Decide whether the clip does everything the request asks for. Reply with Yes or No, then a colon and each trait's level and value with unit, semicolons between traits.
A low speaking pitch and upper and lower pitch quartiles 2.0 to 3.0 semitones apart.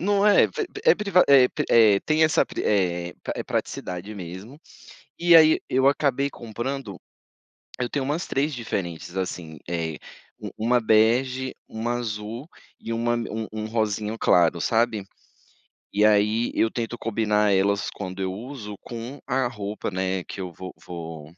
No: low, 110 Hz; average, 5.2 semitones